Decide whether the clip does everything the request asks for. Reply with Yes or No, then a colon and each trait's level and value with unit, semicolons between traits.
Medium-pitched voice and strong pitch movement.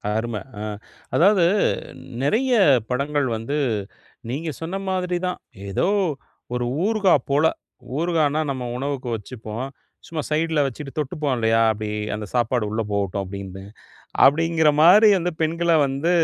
Yes: medium, 145 Hz; wide, 6.3 semitones